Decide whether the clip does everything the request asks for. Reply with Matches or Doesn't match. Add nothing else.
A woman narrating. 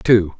Doesn't match